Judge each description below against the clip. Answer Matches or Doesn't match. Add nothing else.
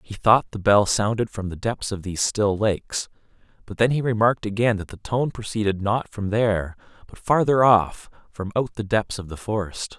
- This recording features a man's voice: Matches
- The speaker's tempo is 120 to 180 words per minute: Doesn't match